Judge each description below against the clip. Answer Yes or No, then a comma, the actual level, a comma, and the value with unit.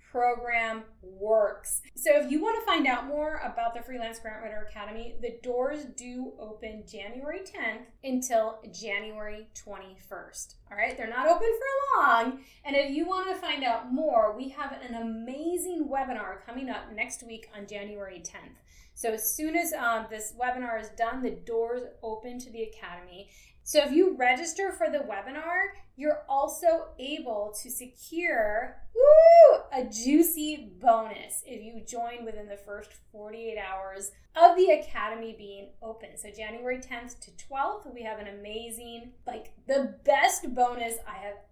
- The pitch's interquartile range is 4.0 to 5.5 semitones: Yes, average, 5.1 semitones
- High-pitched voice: Yes, high, 240 Hz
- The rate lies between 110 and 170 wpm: Yes, average, 160 wpm